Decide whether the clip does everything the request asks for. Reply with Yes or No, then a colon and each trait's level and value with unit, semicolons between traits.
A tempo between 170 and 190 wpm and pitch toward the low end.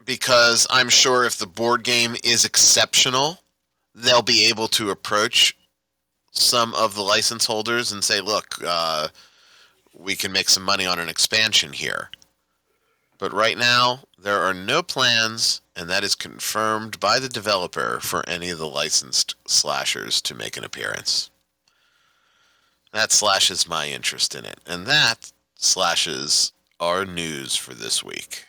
No: average, 145 wpm; low, 100 Hz